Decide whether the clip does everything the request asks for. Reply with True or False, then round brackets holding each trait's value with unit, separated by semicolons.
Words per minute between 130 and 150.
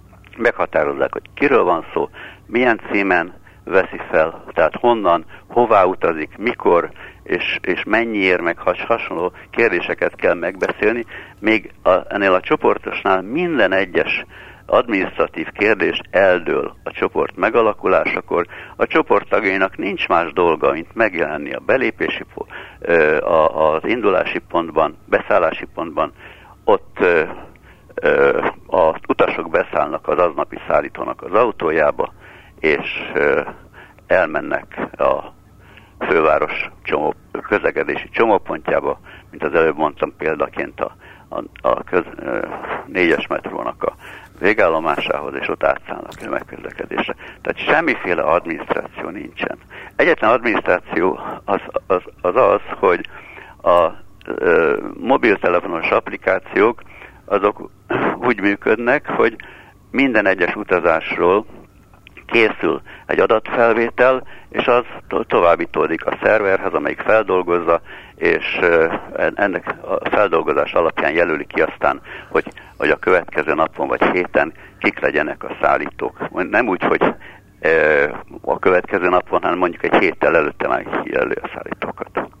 False (110 wpm)